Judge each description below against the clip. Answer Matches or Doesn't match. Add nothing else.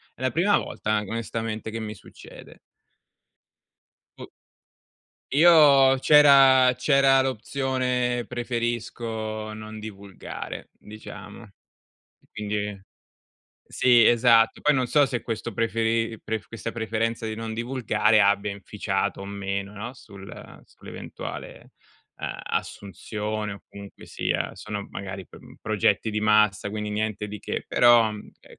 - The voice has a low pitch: Matches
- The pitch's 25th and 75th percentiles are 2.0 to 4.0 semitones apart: Matches